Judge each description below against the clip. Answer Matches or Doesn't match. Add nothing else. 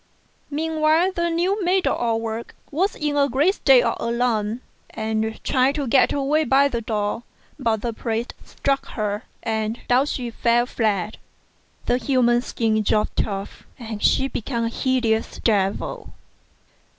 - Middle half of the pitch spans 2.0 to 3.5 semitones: Doesn't match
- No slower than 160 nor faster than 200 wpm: Doesn't match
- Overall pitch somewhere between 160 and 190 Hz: Doesn't match